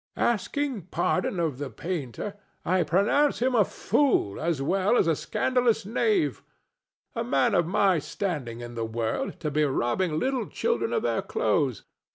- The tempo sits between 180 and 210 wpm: No, average, 160 wpm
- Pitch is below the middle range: No, medium, 185 Hz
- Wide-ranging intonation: Yes, wide, 8.4 semitones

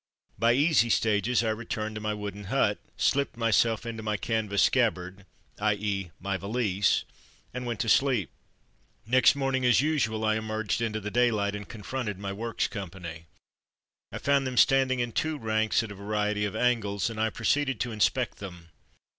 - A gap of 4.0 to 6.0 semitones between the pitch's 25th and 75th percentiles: No, average, 3.0 semitones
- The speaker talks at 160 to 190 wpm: Yes, average, 180 wpm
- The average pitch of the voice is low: Yes, low, 110 Hz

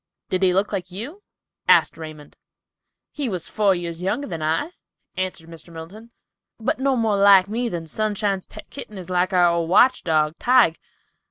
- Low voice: No, medium, 185 Hz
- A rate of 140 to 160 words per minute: No, average, 175 wpm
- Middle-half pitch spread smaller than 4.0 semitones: No, average, 4.4 semitones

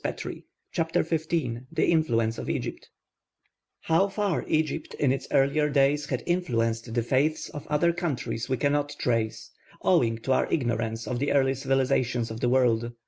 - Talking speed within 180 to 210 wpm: No, average, 155 wpm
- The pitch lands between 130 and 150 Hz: Yes, low, 135 Hz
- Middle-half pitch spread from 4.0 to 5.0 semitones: Yes, average, 4.7 semitones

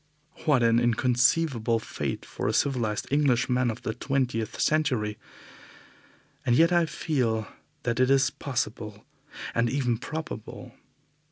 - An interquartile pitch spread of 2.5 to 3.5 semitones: Yes, average, 3.2 semitones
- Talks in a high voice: No, low, 125 Hz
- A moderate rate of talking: No, slow, 120 wpm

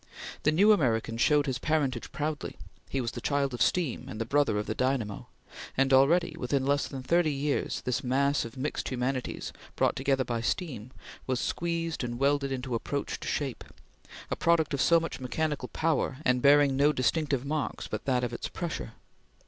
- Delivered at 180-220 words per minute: Yes, average, 185 wpm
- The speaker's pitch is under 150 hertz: Yes, low, 135 Hz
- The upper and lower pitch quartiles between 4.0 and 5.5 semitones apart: No, average, 3.2 semitones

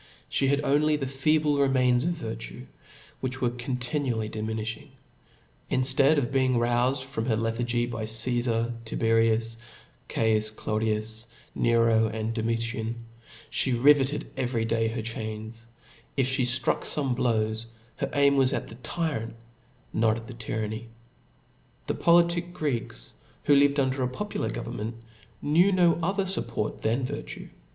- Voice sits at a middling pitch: No, low, 120 Hz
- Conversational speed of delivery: Yes, average, 145 wpm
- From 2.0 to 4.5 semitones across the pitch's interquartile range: Yes, average, 3.4 semitones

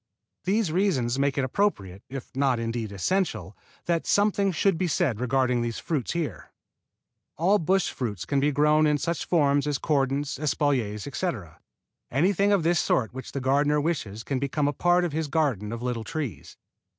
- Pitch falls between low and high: Yes, medium, 145 Hz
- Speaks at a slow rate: No, average, 175 wpm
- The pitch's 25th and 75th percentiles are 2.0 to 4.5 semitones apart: No, average, 5.3 semitones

